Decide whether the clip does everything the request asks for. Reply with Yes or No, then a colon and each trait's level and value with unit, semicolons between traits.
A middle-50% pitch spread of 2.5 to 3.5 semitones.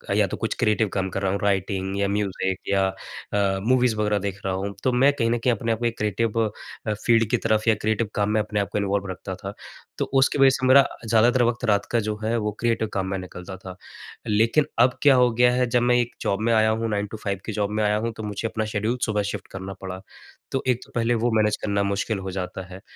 Yes: average, 2.9 semitones